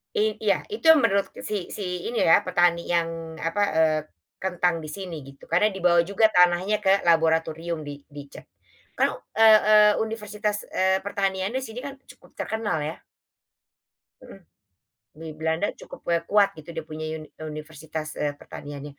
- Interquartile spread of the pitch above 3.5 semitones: Yes, average, 4.2 semitones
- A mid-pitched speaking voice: Yes, medium, 175 Hz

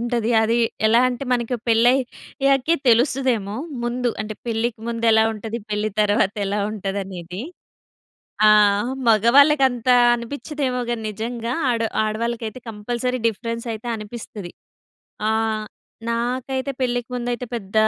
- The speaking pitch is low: No, high, 235 Hz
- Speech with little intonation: Yes, narrow, 2.3 semitones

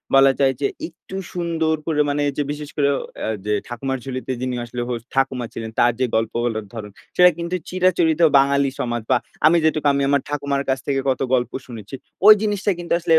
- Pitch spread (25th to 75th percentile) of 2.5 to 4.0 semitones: No, average, 4.5 semitones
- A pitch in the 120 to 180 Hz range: Yes, medium, 140 Hz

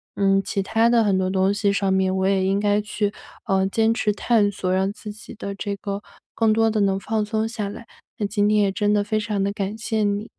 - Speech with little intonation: Yes, narrow, 1.8 semitones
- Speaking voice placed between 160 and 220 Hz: Yes, high, 205 Hz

